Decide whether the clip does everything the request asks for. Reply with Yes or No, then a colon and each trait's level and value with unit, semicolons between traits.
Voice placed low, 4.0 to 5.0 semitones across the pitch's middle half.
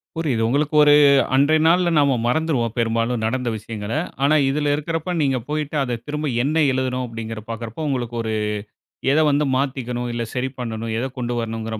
Yes: low, 130 Hz; average, 4.4 semitones